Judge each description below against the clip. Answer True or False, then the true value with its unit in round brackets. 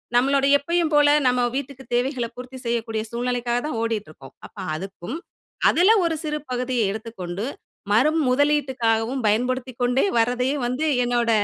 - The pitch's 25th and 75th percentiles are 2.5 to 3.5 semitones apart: True (2.9 semitones)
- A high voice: True (245 Hz)